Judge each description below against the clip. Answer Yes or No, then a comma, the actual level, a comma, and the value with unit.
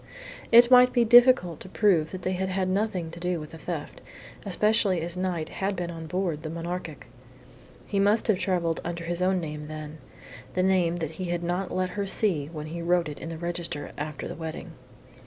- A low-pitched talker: No, medium, 175 Hz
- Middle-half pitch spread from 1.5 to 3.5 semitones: Yes, average, 2.7 semitones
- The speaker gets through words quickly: Yes, fast, 210 wpm